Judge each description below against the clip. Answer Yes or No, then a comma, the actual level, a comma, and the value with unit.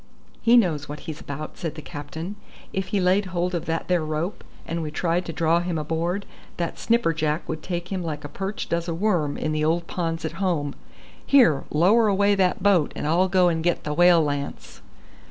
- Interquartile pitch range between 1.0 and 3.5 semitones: Yes, average, 3.0 semitones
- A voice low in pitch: No, medium, 170 Hz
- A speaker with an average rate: No, fast, 210 wpm